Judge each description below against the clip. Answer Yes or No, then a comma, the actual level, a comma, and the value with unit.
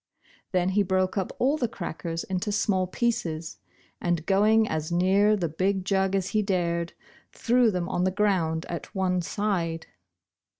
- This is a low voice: No, medium, 185 Hz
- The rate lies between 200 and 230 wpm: No, average, 160 wpm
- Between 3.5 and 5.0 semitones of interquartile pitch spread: No, average, 3.1 semitones